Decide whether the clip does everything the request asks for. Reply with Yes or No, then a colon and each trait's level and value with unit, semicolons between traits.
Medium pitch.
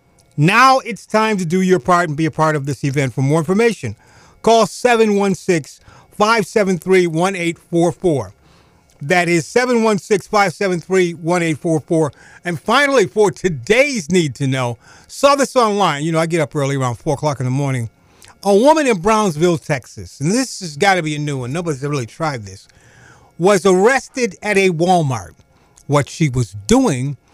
Yes: medium, 170 Hz